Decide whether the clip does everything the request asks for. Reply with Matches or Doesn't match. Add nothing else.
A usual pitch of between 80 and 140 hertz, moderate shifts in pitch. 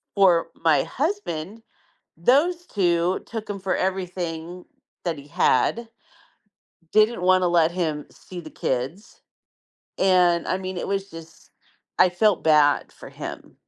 Doesn't match